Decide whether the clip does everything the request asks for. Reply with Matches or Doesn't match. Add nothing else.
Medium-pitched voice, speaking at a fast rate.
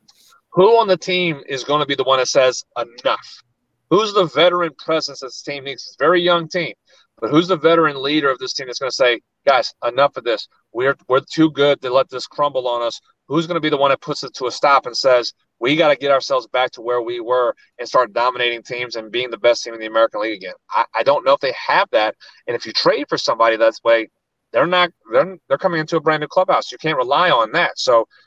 Matches